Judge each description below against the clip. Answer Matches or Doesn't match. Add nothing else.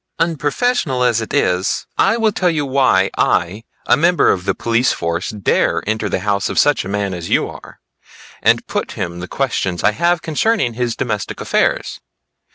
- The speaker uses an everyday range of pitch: Doesn't match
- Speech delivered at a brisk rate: Doesn't match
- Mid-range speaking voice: Doesn't match